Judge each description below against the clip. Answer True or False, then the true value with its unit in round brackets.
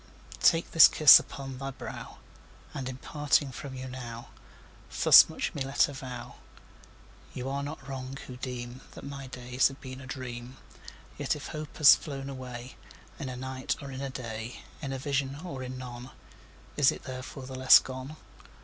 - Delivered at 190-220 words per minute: False (175 wpm)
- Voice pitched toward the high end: False (130 Hz)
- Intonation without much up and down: True (1.4 semitones)